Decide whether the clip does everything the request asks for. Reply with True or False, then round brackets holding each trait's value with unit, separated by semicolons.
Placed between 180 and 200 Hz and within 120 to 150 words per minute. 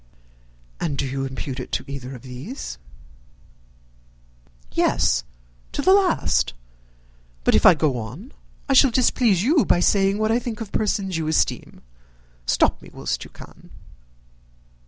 True (185 Hz; 145 wpm)